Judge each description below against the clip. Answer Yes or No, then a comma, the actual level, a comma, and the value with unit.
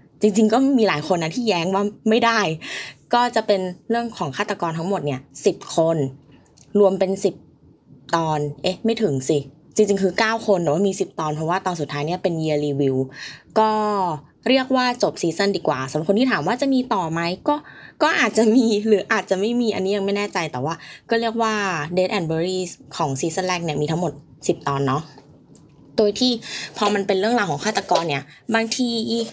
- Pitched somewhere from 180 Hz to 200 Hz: Yes, high, 190 Hz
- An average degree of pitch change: No, wide, 6.1 semitones